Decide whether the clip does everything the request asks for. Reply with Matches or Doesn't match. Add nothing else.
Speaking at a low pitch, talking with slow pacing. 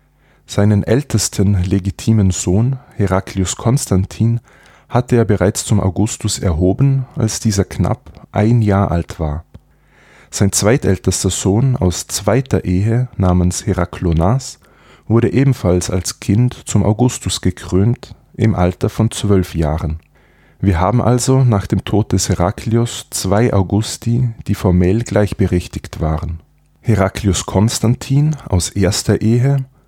Matches